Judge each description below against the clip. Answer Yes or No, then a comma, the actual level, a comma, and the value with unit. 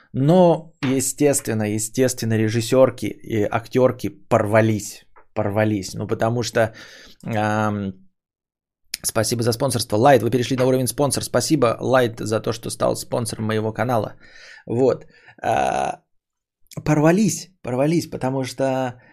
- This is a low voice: Yes, low, 120 Hz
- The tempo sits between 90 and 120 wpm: Yes, average, 115 wpm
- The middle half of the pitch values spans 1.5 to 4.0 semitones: Yes, average, 3.3 semitones